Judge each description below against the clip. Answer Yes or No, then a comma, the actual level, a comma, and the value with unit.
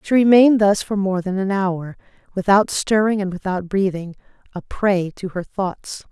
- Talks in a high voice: Yes, high, 195 Hz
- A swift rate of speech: No, average, 175 wpm